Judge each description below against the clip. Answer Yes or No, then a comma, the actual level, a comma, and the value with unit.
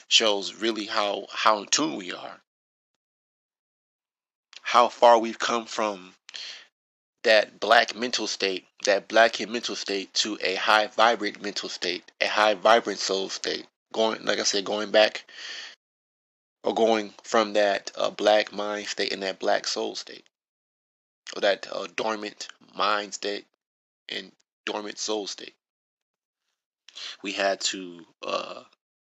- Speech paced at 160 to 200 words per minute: No, slow, 135 wpm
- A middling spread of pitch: No, narrow, 2.0 semitones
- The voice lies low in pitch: Yes, low, 105 Hz